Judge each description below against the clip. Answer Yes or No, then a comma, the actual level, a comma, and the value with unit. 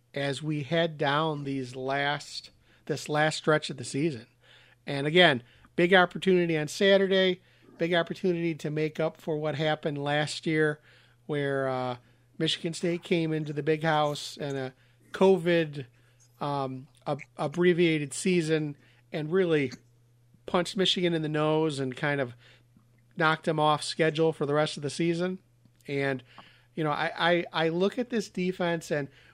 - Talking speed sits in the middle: Yes, average, 155 wpm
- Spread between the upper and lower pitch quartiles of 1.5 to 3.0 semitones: No, average, 3.8 semitones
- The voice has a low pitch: No, medium, 155 Hz